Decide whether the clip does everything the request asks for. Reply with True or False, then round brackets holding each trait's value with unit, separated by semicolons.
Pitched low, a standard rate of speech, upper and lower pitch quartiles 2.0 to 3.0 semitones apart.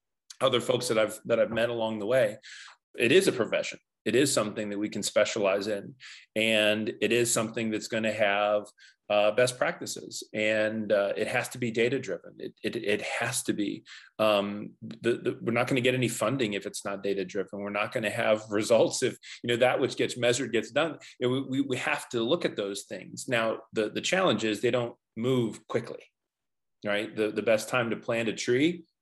False (110 Hz; 220 wpm; 2.7 semitones)